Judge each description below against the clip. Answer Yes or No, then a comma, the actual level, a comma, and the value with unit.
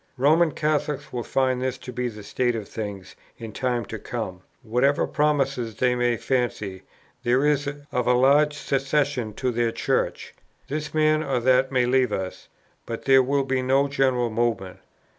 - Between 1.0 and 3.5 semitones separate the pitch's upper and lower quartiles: Yes, average, 2.8 semitones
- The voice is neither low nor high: No, low, 130 Hz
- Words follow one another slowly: No, average, 170 wpm